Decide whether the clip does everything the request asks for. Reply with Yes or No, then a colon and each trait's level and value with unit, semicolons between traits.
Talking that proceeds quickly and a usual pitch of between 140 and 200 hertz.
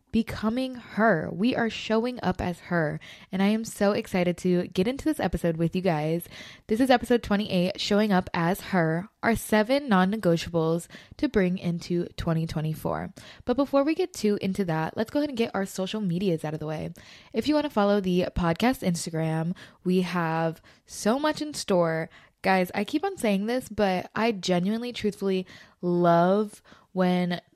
No: average, 180 wpm; high, 190 Hz